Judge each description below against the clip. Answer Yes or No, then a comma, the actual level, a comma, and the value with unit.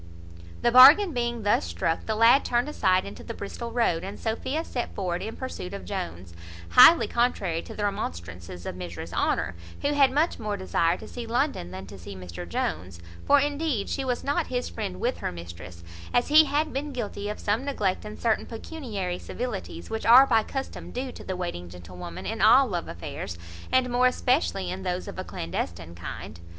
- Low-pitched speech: No, high, 205 Hz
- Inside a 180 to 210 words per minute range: Yes, average, 195 wpm